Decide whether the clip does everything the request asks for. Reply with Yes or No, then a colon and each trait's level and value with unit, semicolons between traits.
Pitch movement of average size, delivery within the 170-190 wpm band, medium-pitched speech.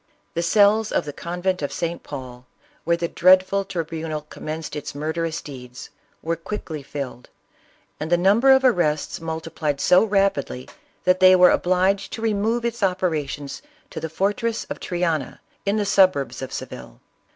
No: average, 4.5 semitones; average, 160 wpm; medium, 170 Hz